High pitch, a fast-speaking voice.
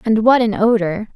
Yes: high, 215 Hz; fast, 210 wpm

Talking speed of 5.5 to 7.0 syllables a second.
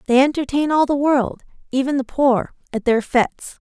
No: 5.1 syllables/s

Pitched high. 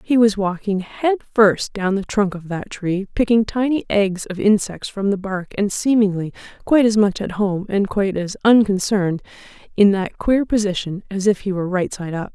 Yes: high, 200 Hz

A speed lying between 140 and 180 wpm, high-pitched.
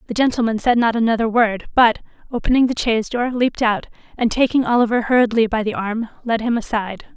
No: average, 195 wpm; high, 230 Hz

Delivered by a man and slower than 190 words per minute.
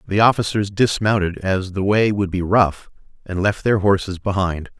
Yes: male; average, 175 wpm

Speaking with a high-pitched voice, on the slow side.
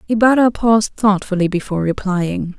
Yes: high, 200 Hz; slow, 115 wpm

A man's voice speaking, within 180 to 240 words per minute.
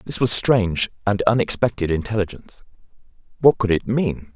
No: male; average, 140 wpm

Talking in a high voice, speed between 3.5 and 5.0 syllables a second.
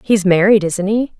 Yes: high, 200 Hz; 4.6 syllables/s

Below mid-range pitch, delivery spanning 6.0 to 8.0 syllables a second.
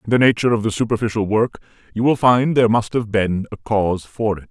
Yes: low, 110 Hz; 6.4 syllables/s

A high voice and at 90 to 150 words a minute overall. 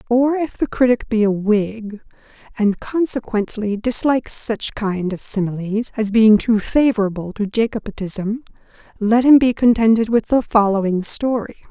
Yes: high, 220 Hz; average, 145 wpm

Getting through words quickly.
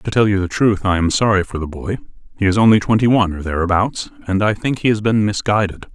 Yes: fast, 240 wpm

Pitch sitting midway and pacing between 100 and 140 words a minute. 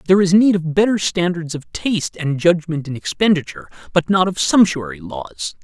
No: medium, 165 Hz; average, 180 wpm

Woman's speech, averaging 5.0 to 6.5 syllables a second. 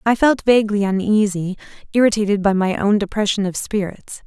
Yes: female; 5.6 syllables/s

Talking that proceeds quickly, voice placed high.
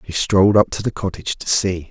No: fast, 250 wpm; very low, 95 Hz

